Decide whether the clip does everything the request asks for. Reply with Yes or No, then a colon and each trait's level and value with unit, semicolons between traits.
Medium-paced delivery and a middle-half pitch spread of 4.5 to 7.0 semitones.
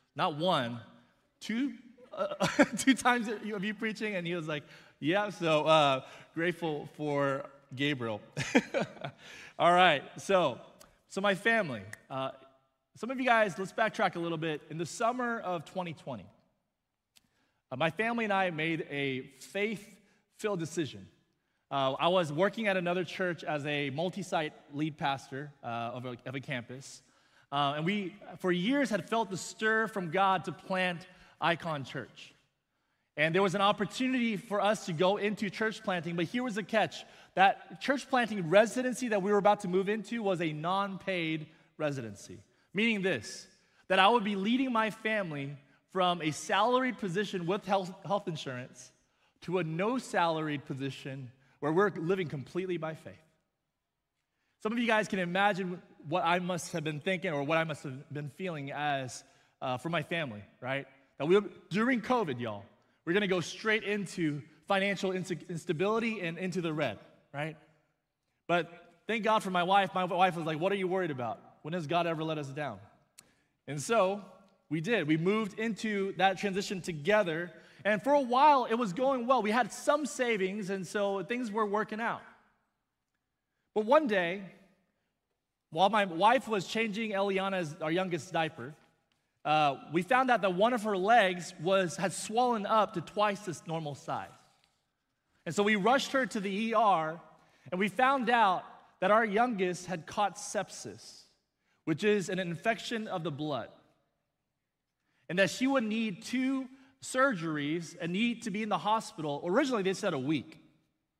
Yes: average, 170 wpm; wide, 5.4 semitones